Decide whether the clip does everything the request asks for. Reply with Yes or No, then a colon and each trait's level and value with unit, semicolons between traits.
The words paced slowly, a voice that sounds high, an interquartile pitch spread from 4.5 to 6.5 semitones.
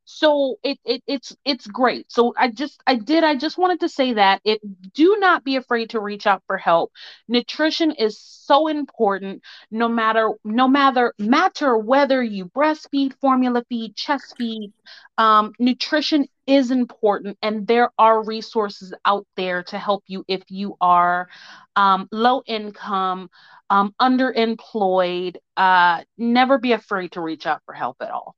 No: average, 160 wpm; high, 230 Hz; average, 5.2 semitones